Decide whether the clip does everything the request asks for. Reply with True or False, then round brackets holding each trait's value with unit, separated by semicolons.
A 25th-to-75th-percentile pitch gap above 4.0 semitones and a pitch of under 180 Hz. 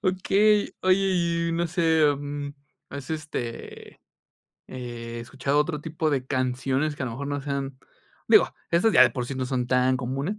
False (3.7 semitones; 140 Hz)